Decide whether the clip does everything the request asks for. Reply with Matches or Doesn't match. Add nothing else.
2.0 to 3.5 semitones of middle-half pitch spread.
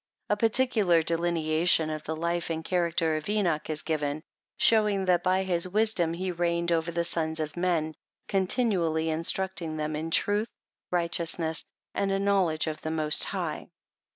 Matches